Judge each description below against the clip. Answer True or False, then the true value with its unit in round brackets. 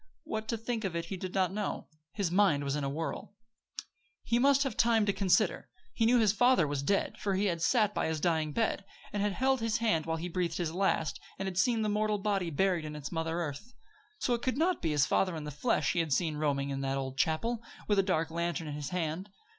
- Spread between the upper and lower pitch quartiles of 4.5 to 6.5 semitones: True (5.3 semitones)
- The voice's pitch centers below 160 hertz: False (185 Hz)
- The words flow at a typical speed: False (250 wpm)